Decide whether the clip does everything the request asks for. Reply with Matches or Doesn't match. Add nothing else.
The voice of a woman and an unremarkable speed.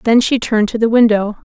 Doesn't match